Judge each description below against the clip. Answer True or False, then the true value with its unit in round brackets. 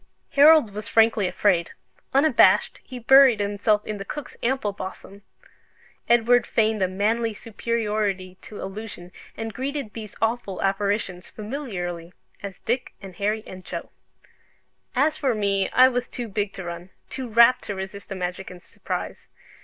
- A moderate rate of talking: True (150 wpm)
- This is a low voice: False (210 Hz)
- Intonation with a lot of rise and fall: False (3.4 semitones)